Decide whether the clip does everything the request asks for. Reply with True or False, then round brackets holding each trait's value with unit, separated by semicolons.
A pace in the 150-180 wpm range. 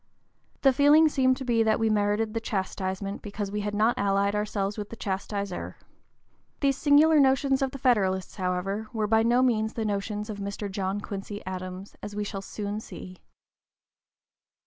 True (170 wpm)